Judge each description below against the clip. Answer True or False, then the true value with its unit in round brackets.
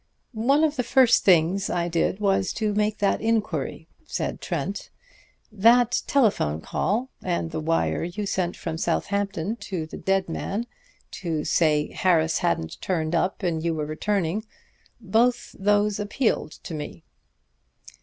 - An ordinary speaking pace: True (145 wpm)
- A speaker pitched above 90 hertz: True (190 Hz)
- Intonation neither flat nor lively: True (4.5 semitones)